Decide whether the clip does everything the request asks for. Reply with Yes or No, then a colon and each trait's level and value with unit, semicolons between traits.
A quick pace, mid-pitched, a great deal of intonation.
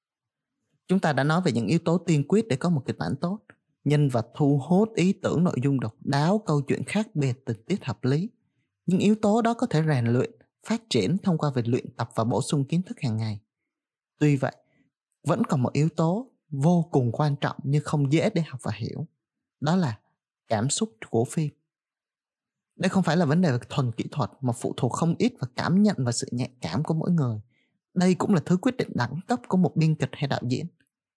No: average, 230 wpm; medium, 150 Hz; wide, 5.8 semitones